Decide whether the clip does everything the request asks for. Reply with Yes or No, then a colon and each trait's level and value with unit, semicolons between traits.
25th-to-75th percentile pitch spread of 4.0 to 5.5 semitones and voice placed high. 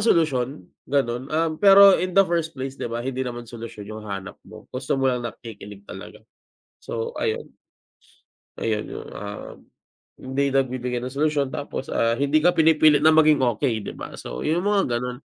No: average, 4.8 semitones; low, 135 Hz